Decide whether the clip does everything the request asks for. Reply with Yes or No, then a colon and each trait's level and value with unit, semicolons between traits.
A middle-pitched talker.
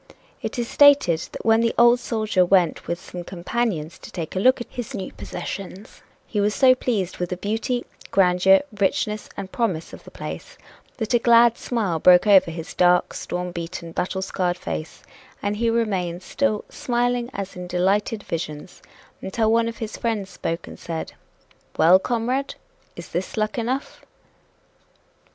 No: high, 200 Hz